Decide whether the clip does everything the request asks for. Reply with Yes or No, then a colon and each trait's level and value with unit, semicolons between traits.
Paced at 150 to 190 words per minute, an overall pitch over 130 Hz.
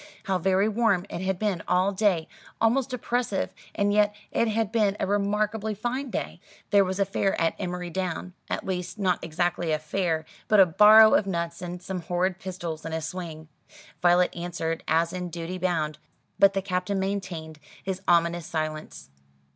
Yes: average, 175 wpm; medium, 185 Hz